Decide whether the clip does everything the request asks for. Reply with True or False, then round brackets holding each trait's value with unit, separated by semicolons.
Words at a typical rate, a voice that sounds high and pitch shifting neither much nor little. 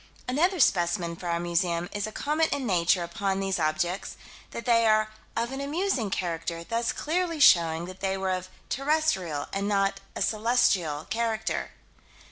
False (160 wpm; 195 Hz; 5.7 semitones)